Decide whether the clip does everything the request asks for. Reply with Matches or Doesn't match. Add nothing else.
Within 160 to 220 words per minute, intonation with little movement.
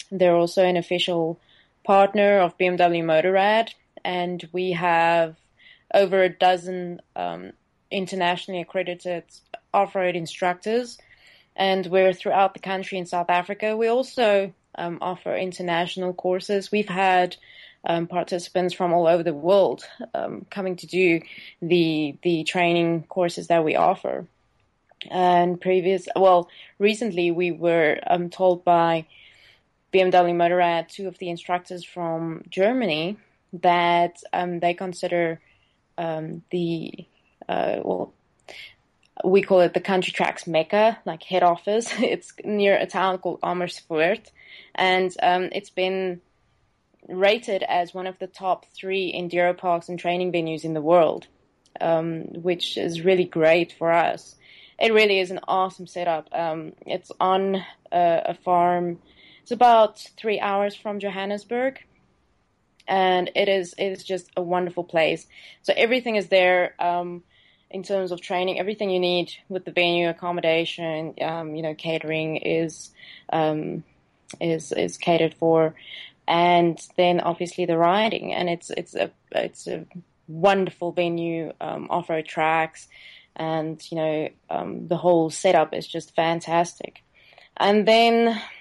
Doesn't match